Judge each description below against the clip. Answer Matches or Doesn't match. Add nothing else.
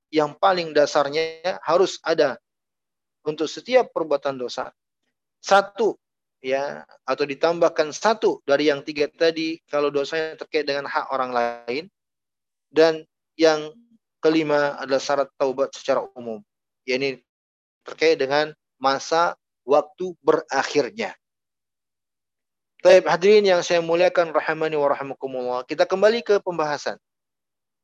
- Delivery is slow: Doesn't match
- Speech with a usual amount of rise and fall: Matches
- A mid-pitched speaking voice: Matches